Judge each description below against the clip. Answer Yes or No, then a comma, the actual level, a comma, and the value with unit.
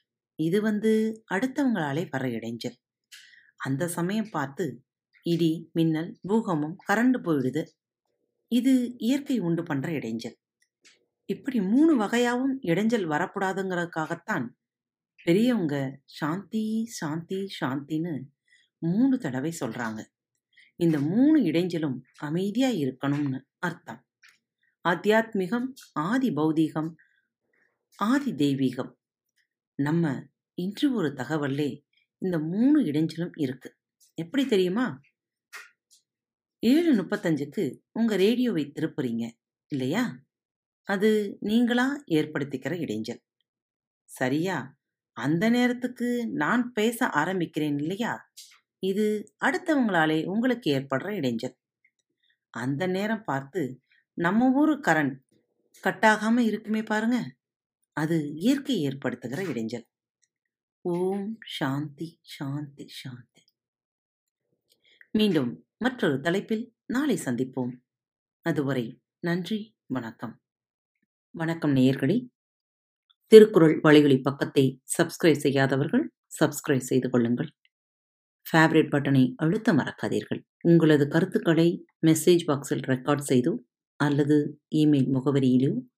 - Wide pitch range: Yes, wide, 7.8 semitones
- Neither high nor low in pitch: Yes, medium, 165 Hz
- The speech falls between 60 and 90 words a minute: Yes, average, 85 wpm